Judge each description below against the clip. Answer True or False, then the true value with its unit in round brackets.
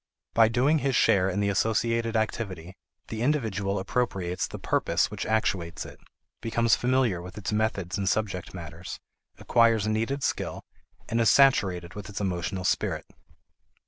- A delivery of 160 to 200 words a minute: False (145 wpm)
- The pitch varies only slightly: False (3.8 semitones)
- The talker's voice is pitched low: True (105 Hz)